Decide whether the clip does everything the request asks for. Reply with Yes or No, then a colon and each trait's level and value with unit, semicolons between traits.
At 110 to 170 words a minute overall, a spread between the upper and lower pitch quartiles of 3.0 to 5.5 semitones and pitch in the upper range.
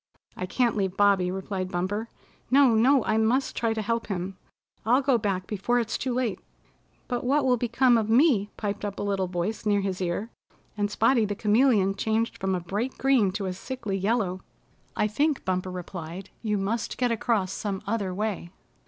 No: average, 190 wpm; average, 3.6 semitones; high, 210 Hz